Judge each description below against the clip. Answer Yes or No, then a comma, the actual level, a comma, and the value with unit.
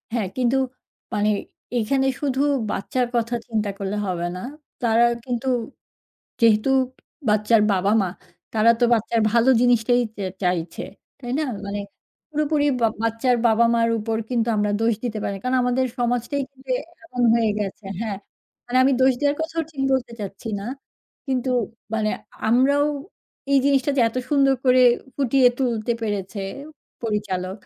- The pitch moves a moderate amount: Yes, average, 3.6 semitones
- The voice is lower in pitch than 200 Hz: No, high, 235 Hz